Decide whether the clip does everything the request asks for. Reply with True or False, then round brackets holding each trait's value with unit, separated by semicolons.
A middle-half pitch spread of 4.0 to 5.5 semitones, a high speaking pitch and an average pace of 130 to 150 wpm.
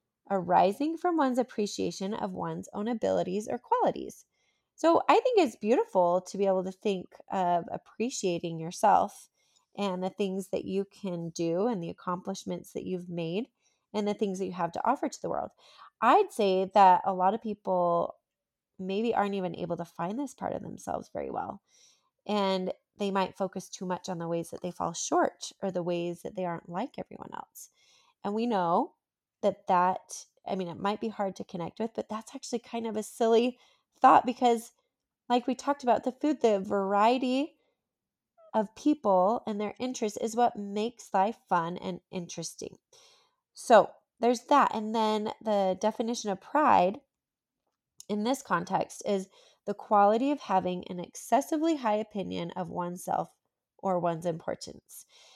False (4.6 semitones; 205 Hz; 170 wpm)